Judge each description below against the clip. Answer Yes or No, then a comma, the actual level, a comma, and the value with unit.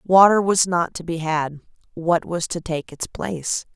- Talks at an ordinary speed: Yes, average, 190 wpm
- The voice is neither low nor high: Yes, medium, 170 Hz